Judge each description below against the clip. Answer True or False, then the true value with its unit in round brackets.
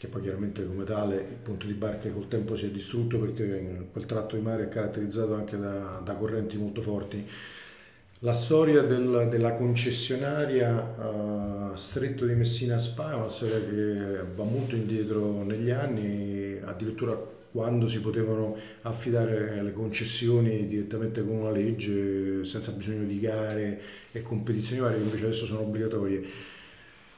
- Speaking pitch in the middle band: False (110 Hz)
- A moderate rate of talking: True (150 wpm)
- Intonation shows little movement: True (2.0 semitones)